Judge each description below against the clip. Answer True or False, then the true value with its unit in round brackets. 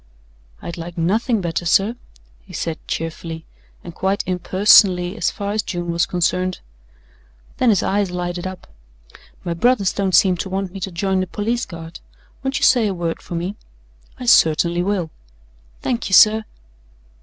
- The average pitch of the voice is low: False (185 Hz)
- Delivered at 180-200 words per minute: False (165 wpm)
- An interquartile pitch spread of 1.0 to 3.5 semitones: True (2.9 semitones)